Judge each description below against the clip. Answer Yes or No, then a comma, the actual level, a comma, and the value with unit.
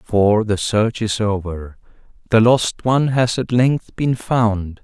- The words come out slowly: No, average, 160 wpm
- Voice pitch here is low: Yes, low, 110 Hz